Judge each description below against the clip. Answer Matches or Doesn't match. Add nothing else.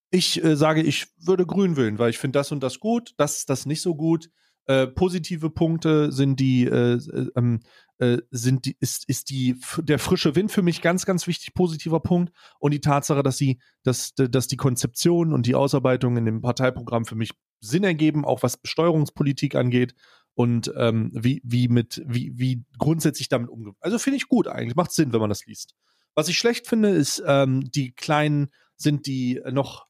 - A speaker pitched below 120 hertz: Doesn't match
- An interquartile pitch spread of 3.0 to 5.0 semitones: Matches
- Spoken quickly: Matches